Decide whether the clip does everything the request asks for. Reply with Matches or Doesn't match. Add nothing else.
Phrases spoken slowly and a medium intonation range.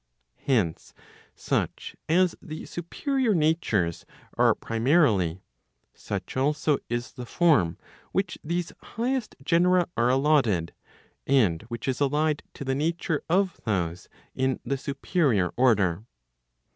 Doesn't match